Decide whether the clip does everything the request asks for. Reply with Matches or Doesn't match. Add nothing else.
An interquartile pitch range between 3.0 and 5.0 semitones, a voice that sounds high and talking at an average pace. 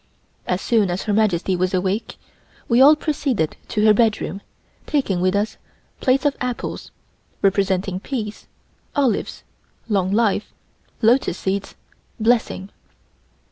Doesn't match